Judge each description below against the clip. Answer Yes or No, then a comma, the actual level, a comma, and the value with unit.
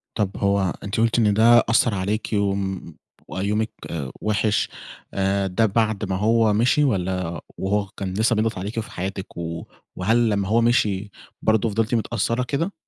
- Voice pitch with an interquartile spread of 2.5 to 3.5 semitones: Yes, average, 2.8 semitones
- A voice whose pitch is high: No, low, 105 Hz